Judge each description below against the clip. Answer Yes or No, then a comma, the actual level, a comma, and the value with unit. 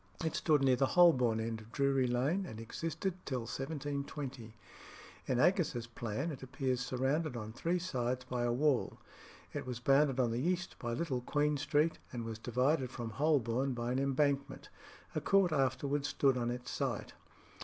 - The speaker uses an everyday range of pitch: Yes, average, 3.4 semitones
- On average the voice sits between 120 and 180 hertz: Yes, low, 135 Hz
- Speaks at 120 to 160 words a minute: No, average, 170 wpm